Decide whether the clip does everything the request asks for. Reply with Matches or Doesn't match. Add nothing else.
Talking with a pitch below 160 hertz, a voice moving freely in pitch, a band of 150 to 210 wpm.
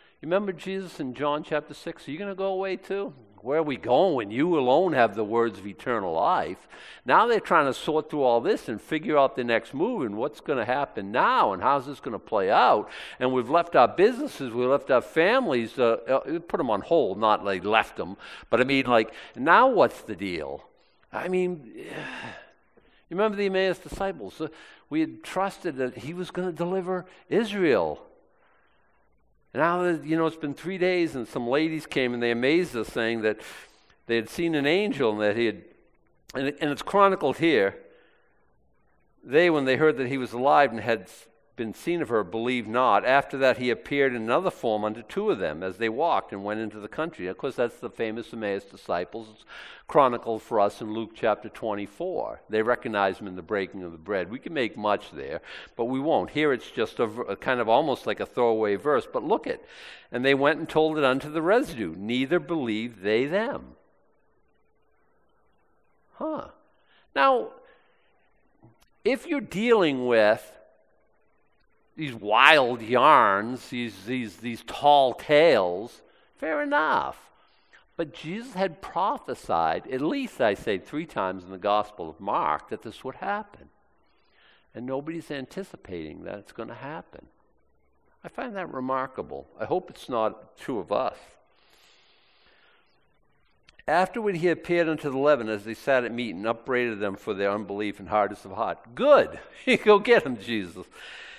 Matches